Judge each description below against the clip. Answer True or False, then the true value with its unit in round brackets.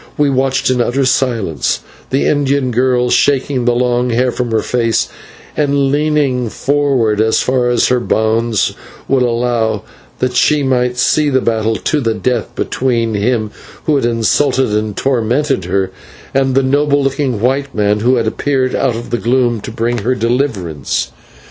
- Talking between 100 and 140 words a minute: False (165 wpm)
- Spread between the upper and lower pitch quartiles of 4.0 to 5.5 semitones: False (2.9 semitones)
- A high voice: False (125 Hz)